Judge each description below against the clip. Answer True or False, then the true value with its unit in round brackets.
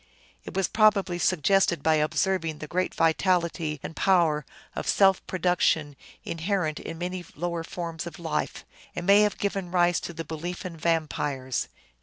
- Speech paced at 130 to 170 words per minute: True (165 wpm)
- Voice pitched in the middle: True (175 Hz)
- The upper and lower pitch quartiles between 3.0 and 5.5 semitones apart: False (2.5 semitones)